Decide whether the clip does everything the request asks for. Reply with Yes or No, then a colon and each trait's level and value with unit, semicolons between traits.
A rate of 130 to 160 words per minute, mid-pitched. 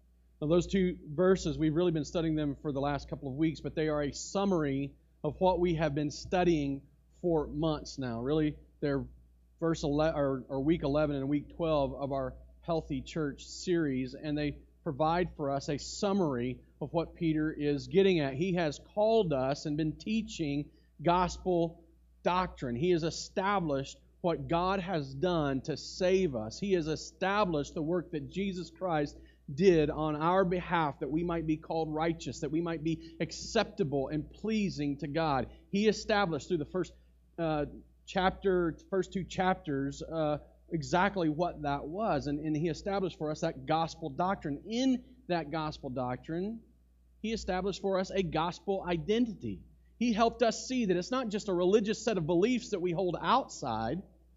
No: average, 170 wpm; medium, 160 Hz